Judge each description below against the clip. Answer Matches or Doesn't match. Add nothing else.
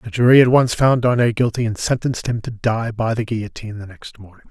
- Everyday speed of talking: Doesn't match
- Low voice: Matches